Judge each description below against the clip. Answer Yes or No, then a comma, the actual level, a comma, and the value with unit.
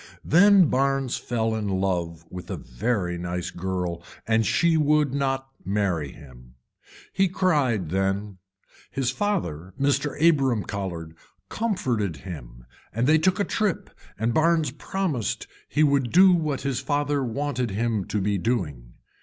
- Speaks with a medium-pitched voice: No, low, 120 Hz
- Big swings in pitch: Yes, wide, 8.0 semitones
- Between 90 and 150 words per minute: Yes, average, 140 wpm